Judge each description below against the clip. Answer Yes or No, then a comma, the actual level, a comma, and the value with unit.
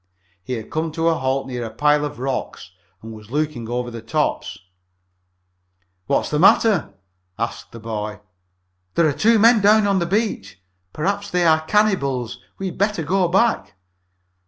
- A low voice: No, medium, 150 Hz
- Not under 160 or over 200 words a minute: Yes, average, 170 wpm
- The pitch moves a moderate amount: No, wide, 8.0 semitones